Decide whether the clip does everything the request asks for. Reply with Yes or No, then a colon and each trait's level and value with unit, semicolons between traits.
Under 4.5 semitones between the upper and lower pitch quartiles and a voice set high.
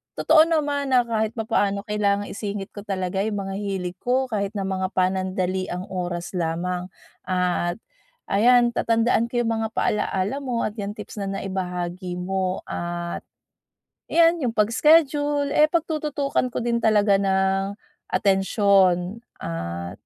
Yes: average, 4.1 semitones; high, 200 Hz